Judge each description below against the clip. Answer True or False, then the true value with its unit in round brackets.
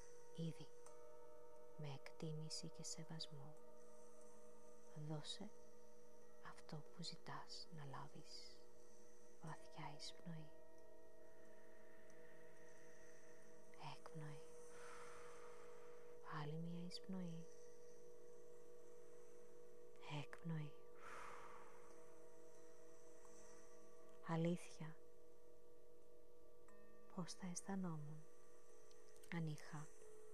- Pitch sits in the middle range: True (160 Hz)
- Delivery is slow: True (45 wpm)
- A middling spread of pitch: False (0.9 semitones)